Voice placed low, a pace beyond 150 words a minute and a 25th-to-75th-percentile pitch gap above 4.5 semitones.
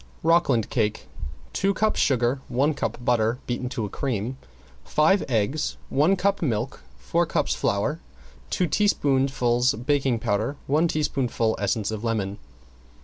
No: low, 125 Hz; slow, 135 wpm; average, 5.0 semitones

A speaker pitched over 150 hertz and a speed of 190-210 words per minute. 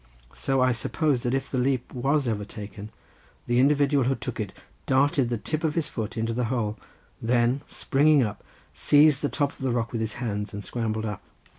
No: low, 125 Hz; average, 200 wpm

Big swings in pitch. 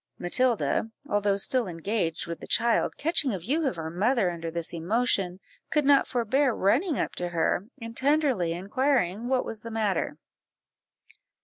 Yes: wide, 6.5 semitones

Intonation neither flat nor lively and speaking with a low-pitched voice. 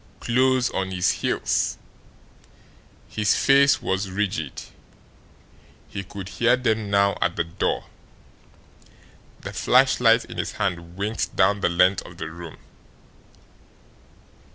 Yes: average, 3.4 semitones; low, 100 Hz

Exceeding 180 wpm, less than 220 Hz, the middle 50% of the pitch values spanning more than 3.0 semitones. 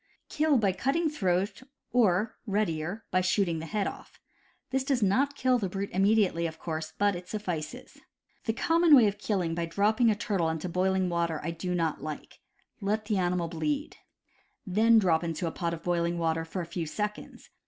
Yes: average, 190 wpm; high, 190 Hz; average, 4.2 semitones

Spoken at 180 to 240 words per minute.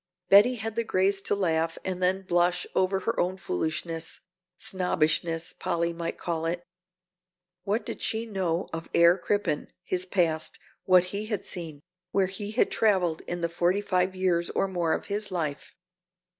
No: average, 165 wpm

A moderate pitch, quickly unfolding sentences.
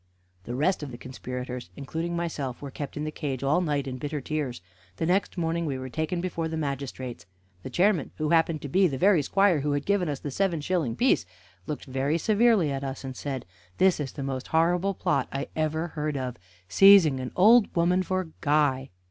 Yes: medium, 150 Hz; fast, 210 wpm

